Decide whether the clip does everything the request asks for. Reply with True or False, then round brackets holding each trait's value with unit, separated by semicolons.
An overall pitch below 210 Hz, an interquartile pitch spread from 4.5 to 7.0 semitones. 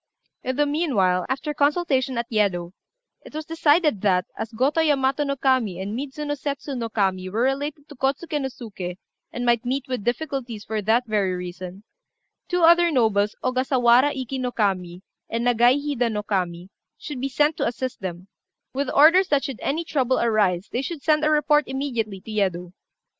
False (250 Hz; 5.6 semitones)